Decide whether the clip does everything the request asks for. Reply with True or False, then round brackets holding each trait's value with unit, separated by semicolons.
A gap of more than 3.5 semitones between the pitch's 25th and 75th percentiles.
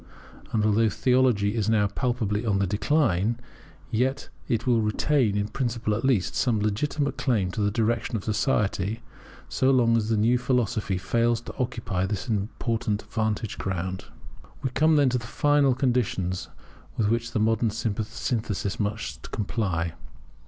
False (3.1 semitones)